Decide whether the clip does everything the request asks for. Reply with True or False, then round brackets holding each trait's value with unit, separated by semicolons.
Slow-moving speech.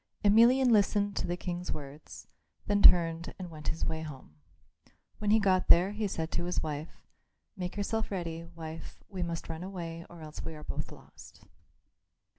False (175 wpm)